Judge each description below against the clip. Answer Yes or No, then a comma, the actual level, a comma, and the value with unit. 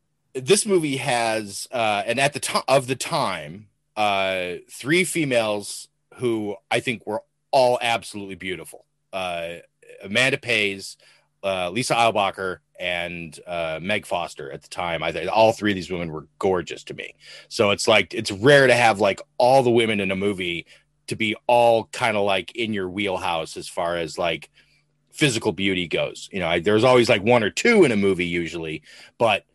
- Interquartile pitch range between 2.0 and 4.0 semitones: No, average, 5.2 semitones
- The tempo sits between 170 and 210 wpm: Yes, average, 185 wpm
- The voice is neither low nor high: No, low, 110 Hz